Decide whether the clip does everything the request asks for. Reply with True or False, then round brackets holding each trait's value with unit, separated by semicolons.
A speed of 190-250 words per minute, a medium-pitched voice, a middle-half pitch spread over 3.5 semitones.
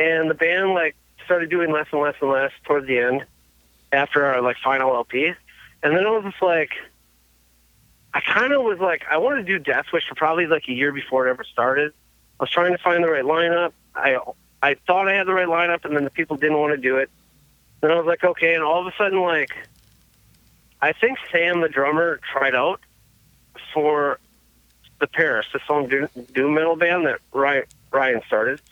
True (205 wpm; 155 Hz; 4.1 semitones)